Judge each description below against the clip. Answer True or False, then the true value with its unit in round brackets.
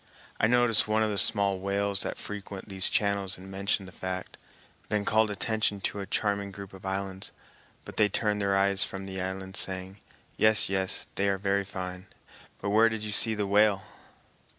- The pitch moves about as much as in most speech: False (1.5 semitones)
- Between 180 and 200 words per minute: True (190 wpm)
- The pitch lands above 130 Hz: False (100 Hz)